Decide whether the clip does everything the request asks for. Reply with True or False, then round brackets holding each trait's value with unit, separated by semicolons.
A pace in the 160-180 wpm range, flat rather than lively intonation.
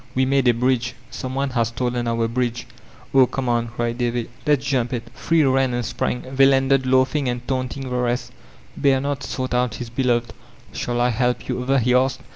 False (200 wpm; 1.7 semitones)